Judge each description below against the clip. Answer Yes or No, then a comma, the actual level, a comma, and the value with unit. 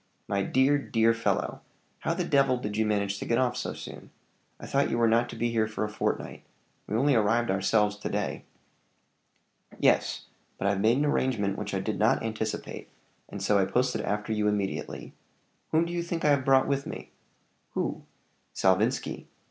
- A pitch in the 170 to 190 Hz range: No, low, 110 Hz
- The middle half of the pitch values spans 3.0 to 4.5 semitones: Yes, average, 3.9 semitones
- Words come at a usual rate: Yes, average, 190 wpm